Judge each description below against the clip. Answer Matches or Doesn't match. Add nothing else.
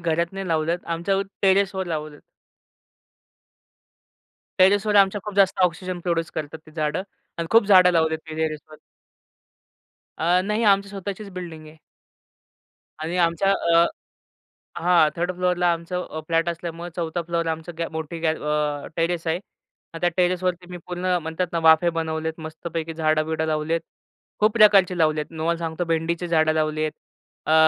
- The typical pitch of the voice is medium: Matches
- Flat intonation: Matches